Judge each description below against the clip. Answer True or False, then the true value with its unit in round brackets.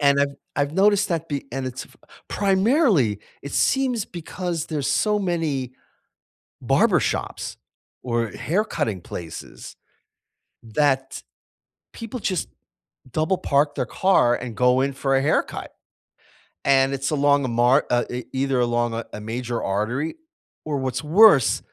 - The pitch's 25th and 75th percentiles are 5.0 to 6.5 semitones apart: True (5.3 semitones)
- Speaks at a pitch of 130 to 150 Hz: True (140 Hz)